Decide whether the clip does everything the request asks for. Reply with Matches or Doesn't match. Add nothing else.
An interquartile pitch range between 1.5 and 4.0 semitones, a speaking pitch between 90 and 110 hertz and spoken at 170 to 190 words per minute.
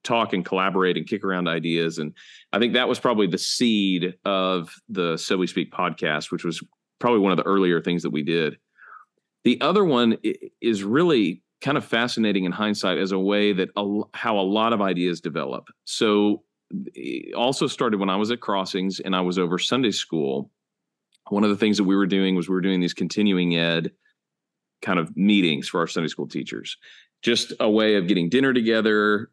Doesn't match